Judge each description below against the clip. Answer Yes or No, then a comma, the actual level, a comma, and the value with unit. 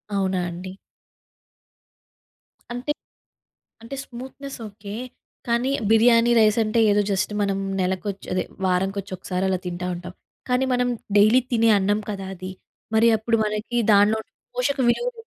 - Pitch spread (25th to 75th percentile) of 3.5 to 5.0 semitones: Yes, average, 3.8 semitones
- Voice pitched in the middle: No, high, 210 Hz